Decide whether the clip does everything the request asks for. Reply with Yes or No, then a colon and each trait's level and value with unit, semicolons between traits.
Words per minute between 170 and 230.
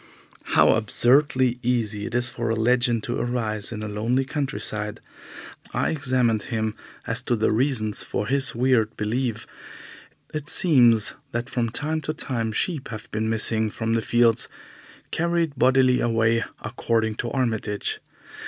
No: average, 145 wpm